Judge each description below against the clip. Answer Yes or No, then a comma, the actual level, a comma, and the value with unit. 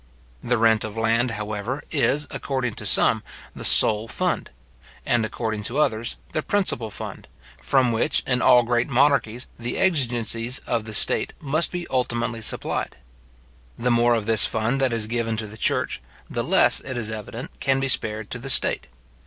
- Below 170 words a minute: No, average, 175 wpm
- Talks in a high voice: No, low, 120 Hz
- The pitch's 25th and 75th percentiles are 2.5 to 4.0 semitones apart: Yes, average, 2.8 semitones